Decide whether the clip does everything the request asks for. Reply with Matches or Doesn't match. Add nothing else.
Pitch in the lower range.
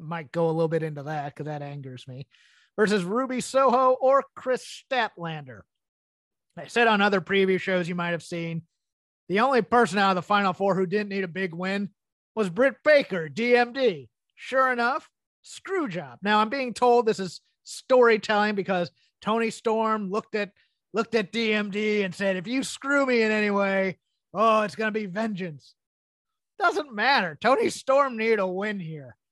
Doesn't match